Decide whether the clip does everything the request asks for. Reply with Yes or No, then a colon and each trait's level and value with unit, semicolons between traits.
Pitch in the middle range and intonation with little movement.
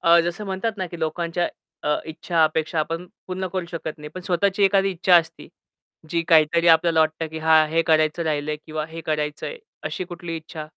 Yes: medium, 165 Hz; narrow, 2.0 semitones